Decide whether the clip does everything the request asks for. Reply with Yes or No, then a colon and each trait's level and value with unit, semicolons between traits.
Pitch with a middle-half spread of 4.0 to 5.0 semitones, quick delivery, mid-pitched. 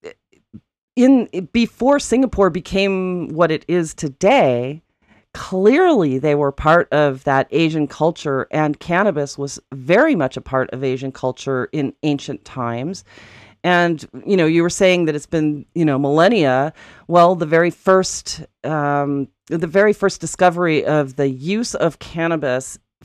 No: average, 4.7 semitones; average, 145 wpm; medium, 155 Hz